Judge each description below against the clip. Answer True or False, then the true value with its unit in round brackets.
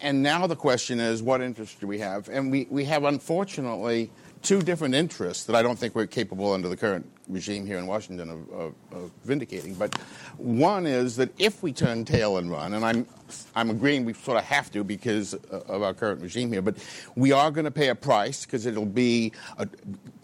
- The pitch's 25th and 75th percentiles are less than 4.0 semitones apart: False (4.7 semitones)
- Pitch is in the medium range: False (120 Hz)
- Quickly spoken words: True (215 wpm)